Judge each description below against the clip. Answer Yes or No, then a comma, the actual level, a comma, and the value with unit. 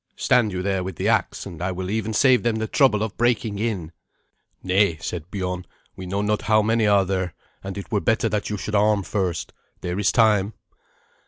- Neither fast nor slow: No, fast, 210 wpm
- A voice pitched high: No, low, 100 Hz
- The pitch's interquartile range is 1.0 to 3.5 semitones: Yes, average, 2.8 semitones